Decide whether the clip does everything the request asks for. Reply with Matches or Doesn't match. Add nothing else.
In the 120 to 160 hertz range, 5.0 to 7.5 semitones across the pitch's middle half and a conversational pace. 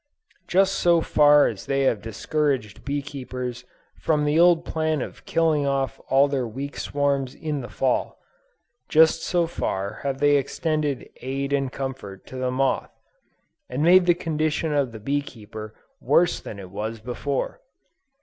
Doesn't match